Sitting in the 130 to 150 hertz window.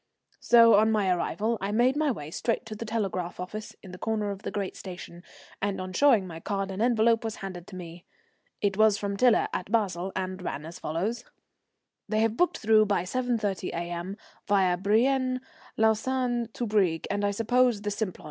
No: high, 205 Hz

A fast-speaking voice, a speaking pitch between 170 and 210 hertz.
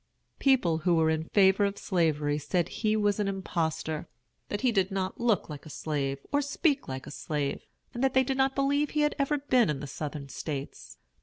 Yes: fast, 210 wpm; high, 190 Hz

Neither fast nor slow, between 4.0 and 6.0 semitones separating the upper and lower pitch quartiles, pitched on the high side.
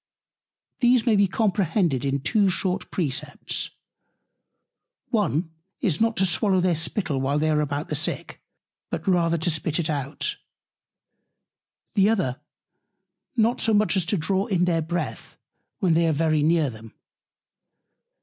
No: average, 145 wpm; average, 4.6 semitones; medium, 170 Hz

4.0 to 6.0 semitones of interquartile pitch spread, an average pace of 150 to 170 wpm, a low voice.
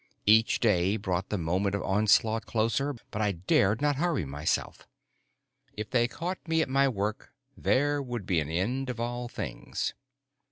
Yes: average, 5.3 semitones; average, 165 wpm; low, 110 Hz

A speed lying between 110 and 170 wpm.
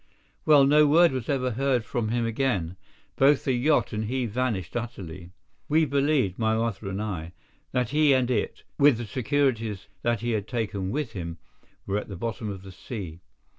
No: average, 185 wpm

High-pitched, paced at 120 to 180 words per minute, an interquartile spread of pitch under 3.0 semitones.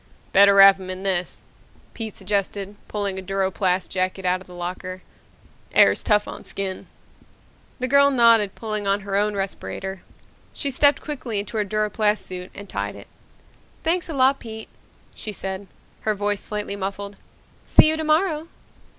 Yes: high, 200 Hz; average, 160 wpm; narrow, 2.6 semitones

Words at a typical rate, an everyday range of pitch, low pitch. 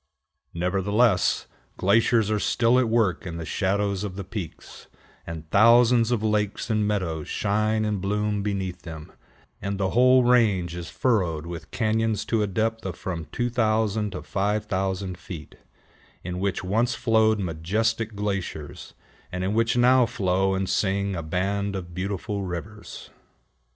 Yes: average, 145 wpm; average, 3.2 semitones; low, 100 Hz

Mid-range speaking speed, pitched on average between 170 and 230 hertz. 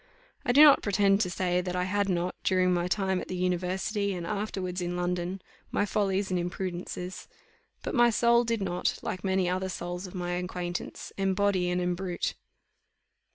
Yes: average, 175 wpm; medium, 185 Hz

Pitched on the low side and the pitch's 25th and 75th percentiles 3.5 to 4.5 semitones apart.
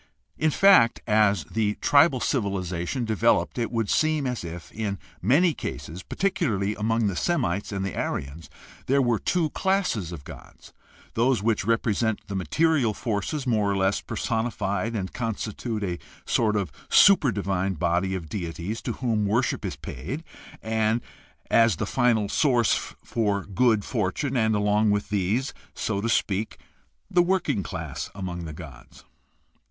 Yes: low, 110 Hz; average, 4.1 semitones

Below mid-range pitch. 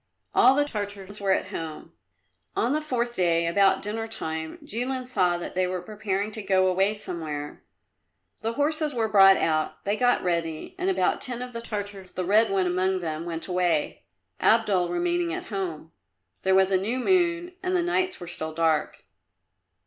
No: high, 195 Hz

